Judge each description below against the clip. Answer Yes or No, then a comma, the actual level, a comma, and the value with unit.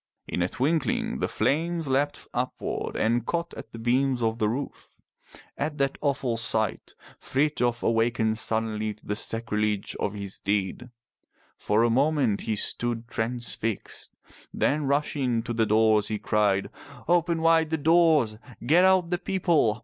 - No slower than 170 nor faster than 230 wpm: No, average, 150 wpm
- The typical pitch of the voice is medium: No, low, 120 Hz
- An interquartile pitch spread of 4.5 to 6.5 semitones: Yes, average, 5.2 semitones